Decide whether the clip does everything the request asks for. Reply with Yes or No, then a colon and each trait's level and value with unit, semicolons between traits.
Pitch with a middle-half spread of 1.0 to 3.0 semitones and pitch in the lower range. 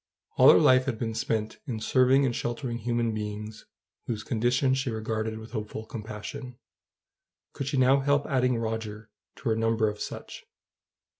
Yes: average, 2.7 semitones; low, 115 Hz